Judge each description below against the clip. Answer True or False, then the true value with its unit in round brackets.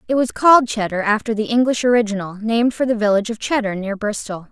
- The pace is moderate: False (210 wpm)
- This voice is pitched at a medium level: False (220 Hz)